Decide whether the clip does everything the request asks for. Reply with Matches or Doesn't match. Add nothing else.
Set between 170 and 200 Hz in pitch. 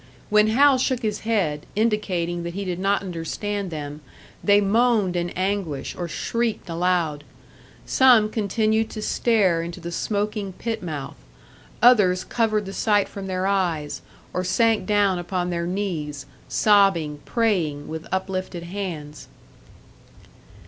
Matches